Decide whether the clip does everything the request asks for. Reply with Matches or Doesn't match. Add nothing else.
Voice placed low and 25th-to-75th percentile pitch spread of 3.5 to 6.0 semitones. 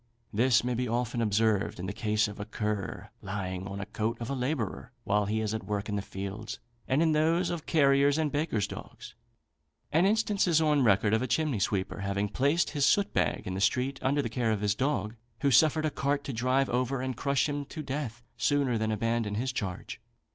Matches